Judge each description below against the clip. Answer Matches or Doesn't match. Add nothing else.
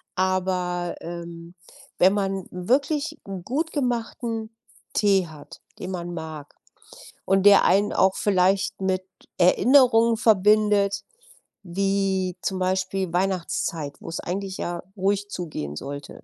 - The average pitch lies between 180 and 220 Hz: Matches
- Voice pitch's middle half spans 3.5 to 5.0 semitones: Doesn't match